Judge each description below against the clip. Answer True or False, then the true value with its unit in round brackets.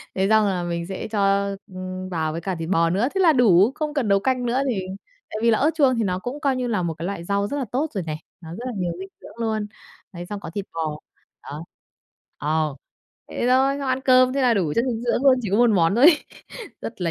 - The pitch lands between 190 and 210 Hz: True (205 Hz)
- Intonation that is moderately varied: False (6.1 semitones)